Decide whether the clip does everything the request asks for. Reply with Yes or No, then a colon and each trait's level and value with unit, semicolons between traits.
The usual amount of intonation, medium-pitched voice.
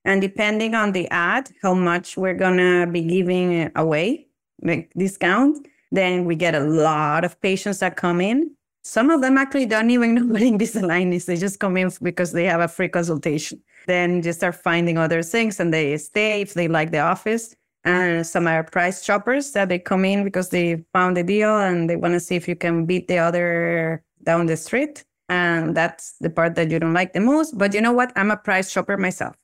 Yes: average, 3.4 semitones; medium, 180 Hz